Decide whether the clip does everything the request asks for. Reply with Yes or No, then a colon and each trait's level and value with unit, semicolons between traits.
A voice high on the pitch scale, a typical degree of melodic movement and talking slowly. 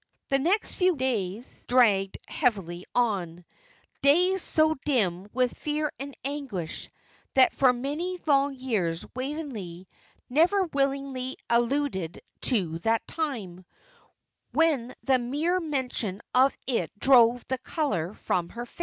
No: very high, 255 Hz; wide, 5.9 semitones; slow, 120 wpm